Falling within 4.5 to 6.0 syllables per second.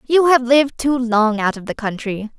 Yes: 5.1 syllables/s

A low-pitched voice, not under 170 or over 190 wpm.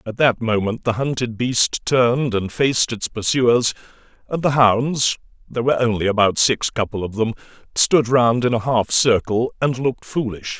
Yes: low, 120 Hz; average, 175 wpm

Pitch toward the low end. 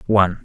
Yes: very low, 95 Hz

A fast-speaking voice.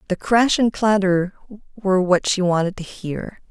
No: average, 170 wpm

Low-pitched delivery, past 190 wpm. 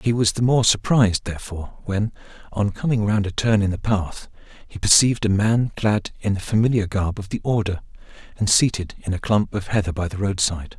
Yes: low, 105 Hz; fast, 205 wpm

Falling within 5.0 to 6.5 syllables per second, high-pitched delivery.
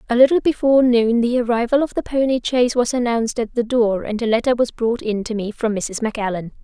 Yes: 6.0 syllables/s; high, 235 Hz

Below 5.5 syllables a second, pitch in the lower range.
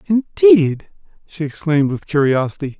No: 4.8 syllables/s; medium, 165 Hz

